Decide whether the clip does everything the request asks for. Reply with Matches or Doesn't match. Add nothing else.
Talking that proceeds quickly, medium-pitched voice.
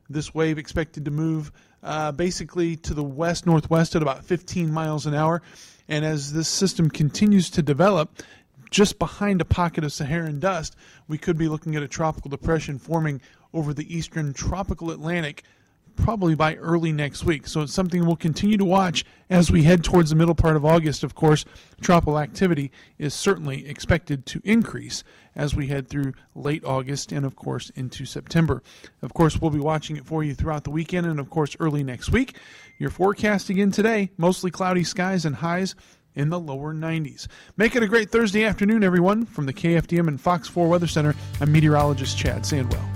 Doesn't match